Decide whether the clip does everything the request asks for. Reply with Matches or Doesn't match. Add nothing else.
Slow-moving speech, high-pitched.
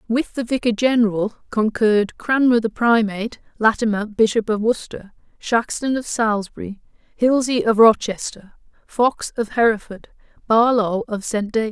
Matches